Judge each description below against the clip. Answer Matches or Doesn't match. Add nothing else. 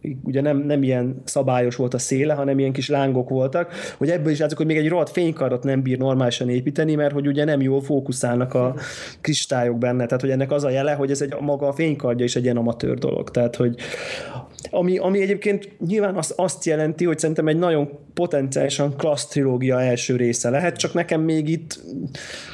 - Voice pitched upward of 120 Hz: Matches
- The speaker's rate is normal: Doesn't match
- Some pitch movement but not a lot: Matches